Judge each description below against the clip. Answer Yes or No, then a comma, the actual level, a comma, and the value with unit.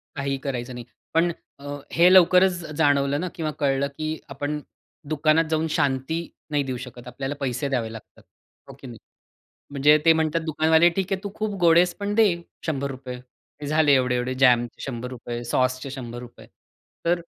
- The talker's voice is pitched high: No, medium, 140 Hz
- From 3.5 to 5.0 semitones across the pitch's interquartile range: Yes, average, 3.9 semitones